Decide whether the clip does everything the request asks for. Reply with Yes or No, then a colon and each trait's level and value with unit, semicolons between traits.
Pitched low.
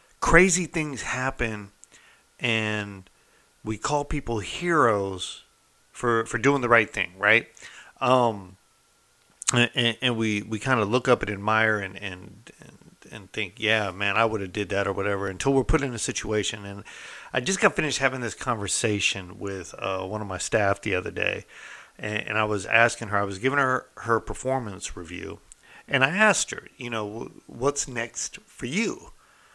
Yes: low, 110 Hz